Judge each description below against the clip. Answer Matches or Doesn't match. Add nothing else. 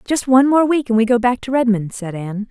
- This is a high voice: Matches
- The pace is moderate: Doesn't match